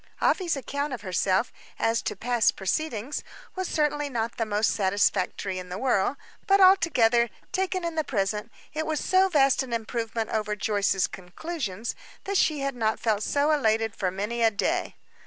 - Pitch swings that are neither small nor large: No, wide, 6.2 semitones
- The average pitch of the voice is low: No, high, 235 Hz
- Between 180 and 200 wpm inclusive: No, average, 170 wpm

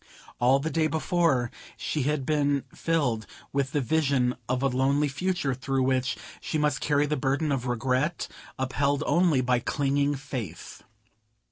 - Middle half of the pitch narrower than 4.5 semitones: Yes, narrow, 2.6 semitones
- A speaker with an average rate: Yes, average, 150 wpm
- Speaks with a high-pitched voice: No, medium, 140 Hz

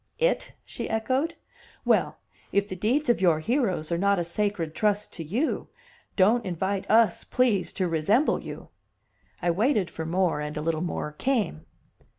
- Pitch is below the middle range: No, high, 195 Hz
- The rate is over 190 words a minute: No, average, 165 wpm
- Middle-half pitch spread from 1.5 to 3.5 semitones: No, average, 5.3 semitones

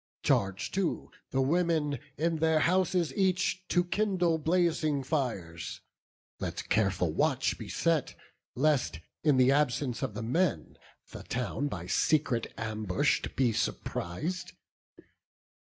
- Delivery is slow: Yes, slow, 120 wpm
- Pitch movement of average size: No, wide, 6.4 semitones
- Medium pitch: Yes, medium, 150 Hz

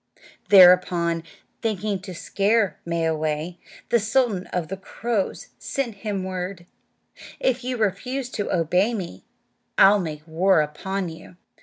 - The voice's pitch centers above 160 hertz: Yes, high, 190 Hz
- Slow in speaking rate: Yes, slow, 125 wpm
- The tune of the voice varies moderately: Yes, average, 4.0 semitones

